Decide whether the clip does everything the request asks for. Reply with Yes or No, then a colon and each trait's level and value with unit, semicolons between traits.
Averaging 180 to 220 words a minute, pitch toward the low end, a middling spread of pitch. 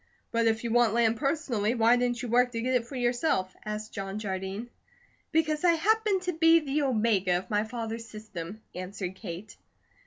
No: average, 185 wpm; high, 230 Hz; average, 4.0 semitones